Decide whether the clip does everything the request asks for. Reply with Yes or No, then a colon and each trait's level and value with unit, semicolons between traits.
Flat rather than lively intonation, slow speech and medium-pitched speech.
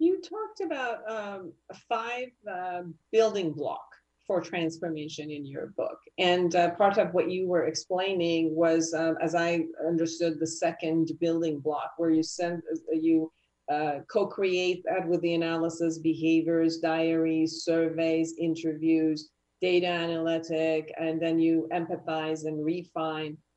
Yes: narrow, 1.7 semitones; slow, 130 wpm; medium, 165 Hz